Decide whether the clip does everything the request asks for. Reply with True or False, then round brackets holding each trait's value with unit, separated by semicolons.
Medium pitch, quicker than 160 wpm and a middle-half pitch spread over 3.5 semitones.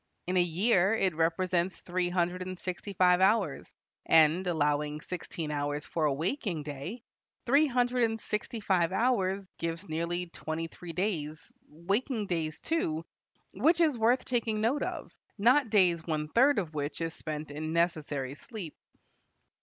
False (180 Hz; 155 wpm; 5.3 semitones)